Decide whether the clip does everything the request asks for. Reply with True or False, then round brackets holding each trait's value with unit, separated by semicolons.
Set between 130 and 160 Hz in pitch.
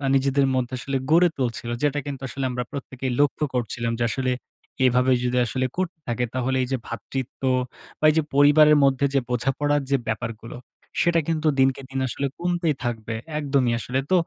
True (135 Hz)